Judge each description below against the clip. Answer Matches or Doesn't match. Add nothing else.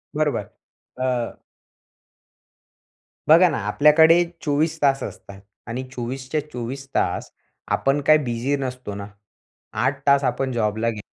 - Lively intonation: Doesn't match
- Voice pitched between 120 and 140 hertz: Matches